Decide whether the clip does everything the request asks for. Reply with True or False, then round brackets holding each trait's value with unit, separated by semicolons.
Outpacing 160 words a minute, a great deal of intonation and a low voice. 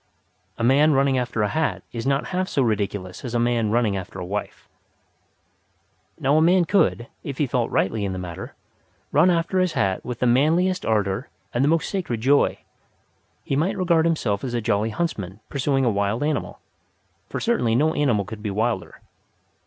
True (185 wpm; 6.6 semitones; 125 Hz)